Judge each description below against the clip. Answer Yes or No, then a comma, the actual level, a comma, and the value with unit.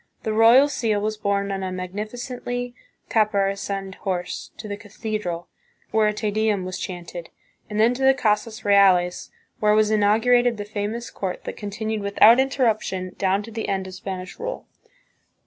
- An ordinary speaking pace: Yes, average, 165 wpm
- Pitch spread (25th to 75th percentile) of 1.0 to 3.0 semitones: Yes, narrow, 2.4 semitones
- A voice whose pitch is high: Yes, high, 210 Hz